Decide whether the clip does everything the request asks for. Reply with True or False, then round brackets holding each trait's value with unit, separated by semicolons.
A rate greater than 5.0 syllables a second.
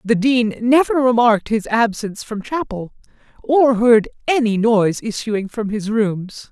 False (4.4 syllables/s)